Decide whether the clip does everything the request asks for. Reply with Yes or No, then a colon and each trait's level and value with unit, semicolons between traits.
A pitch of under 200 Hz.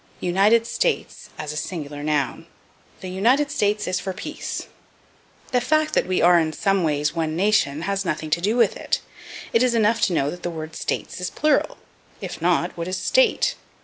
Yes: medium, 185 Hz